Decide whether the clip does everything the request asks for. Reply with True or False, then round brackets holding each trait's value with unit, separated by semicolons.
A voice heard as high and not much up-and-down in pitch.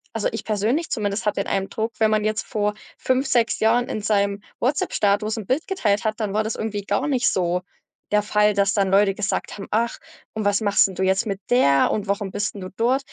True (210 Hz; 2.0 semitones)